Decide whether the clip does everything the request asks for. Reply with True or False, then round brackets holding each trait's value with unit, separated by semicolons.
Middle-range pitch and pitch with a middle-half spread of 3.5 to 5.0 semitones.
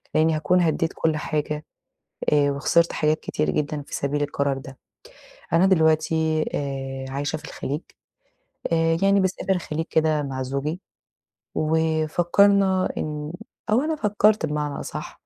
False (155 Hz; 2.5 semitones)